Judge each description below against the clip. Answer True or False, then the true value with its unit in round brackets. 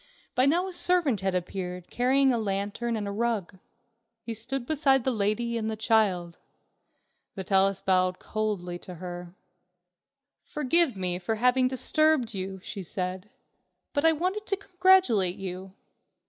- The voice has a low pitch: False (220 Hz)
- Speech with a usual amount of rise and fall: False (6.0 semitones)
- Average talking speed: True (145 wpm)